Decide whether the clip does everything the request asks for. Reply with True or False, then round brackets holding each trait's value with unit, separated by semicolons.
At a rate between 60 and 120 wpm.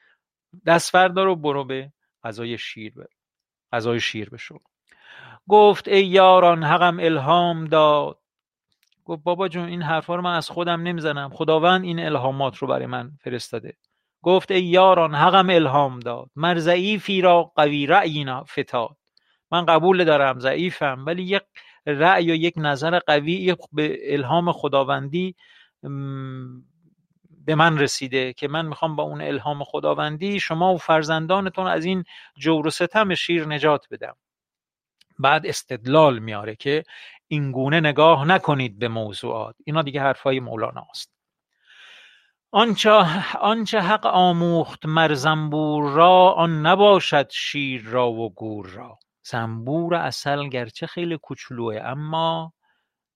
False (130 wpm)